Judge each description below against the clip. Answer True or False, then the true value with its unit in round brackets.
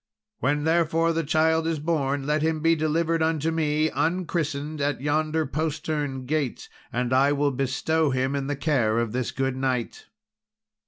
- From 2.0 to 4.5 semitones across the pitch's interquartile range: True (2.9 semitones)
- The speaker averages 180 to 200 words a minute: False (160 wpm)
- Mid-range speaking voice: True (150 Hz)